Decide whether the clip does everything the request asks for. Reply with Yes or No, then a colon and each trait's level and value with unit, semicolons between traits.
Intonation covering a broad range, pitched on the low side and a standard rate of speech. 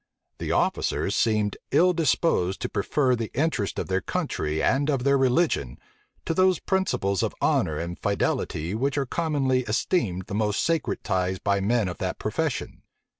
Yes: wide, 7.3 semitones; low, 115 Hz; average, 165 wpm